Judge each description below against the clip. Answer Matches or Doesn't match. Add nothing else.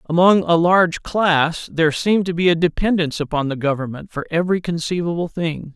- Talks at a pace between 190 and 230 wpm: Doesn't match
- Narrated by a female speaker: Doesn't match